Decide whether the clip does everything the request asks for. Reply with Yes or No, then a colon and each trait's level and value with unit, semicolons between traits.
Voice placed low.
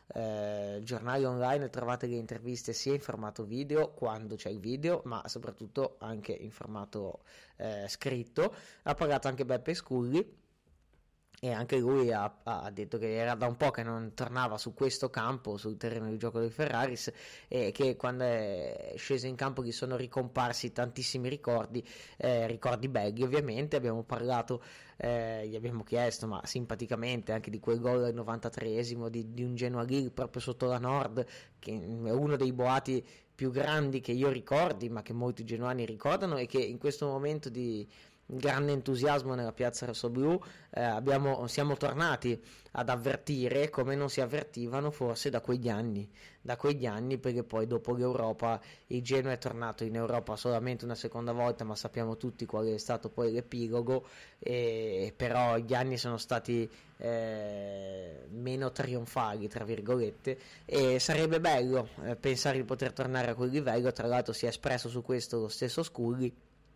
Yes: low, 125 Hz